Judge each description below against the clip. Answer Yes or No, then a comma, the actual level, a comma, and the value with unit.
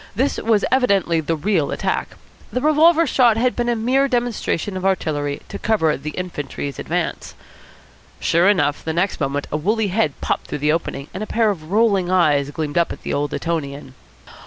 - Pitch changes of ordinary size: No, wide, 6.9 semitones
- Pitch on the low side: No, medium, 185 Hz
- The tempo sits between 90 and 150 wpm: No, average, 185 wpm